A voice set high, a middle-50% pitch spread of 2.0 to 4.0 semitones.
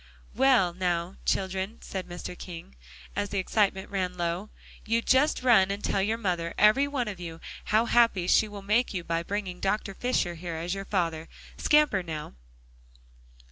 Yes: high, 195 Hz; average, 3.5 semitones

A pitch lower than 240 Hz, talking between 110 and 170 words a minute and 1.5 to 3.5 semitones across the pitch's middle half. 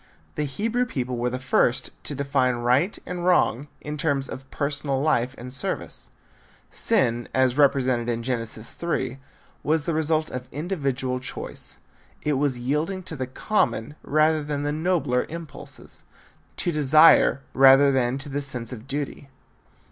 Yes: medium, 140 Hz; average, 150 wpm; average, 3.2 semitones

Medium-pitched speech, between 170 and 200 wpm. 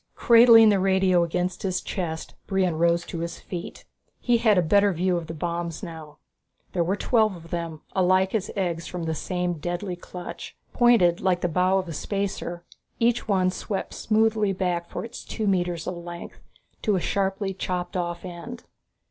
Yes: medium, 180 Hz; average, 180 wpm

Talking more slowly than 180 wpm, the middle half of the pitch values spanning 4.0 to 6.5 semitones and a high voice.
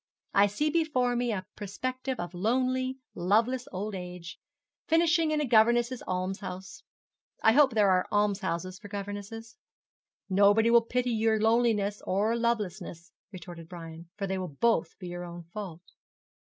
Yes: average, 145 wpm; average, 4.5 semitones; high, 210 Hz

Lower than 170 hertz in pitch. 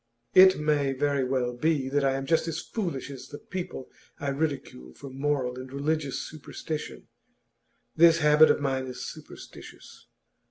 Yes: medium, 140 Hz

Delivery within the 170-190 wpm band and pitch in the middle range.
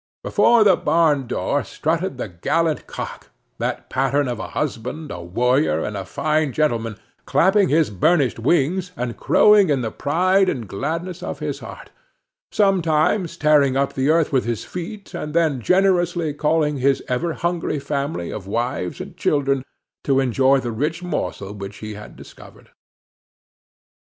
No: average, 155 wpm; medium, 145 Hz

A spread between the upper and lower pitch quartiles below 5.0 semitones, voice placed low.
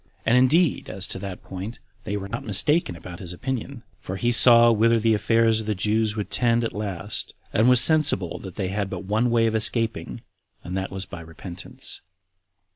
Yes: average, 3.4 semitones; low, 110 Hz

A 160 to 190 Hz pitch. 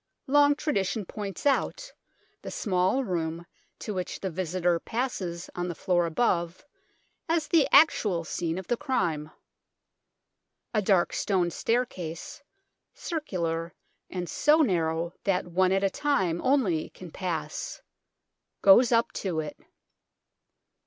Yes: medium, 185 Hz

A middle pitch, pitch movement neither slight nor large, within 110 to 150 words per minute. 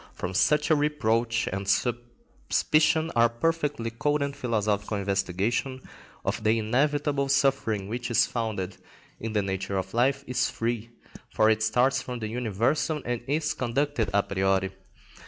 No: low, 120 Hz; average, 4.7 semitones; average, 145 wpm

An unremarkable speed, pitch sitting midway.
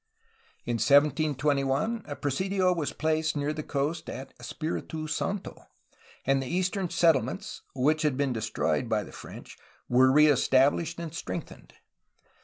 No: slow, 130 wpm; medium, 150 Hz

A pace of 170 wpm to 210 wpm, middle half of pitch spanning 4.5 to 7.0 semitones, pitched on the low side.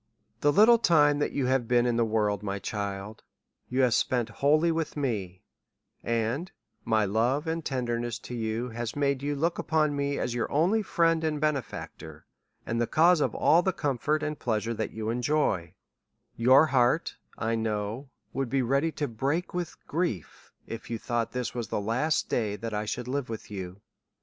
Yes: average, 185 wpm; average, 4.9 semitones; low, 125 Hz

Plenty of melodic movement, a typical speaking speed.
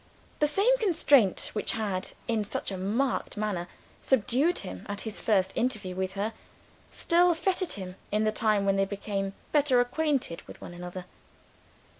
Yes: wide, 6.1 semitones; average, 160 wpm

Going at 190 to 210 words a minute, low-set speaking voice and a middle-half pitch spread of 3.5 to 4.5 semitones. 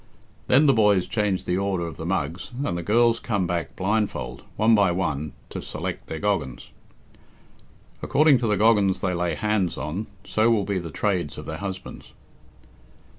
No: average, 175 wpm; very low, 95 Hz; average, 3.8 semitones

